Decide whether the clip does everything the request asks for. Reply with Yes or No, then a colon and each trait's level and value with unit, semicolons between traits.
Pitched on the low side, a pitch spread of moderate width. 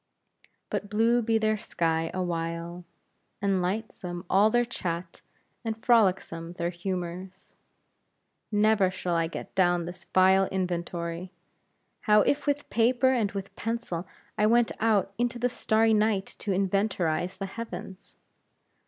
No: high, 190 Hz; average, 3.9 semitones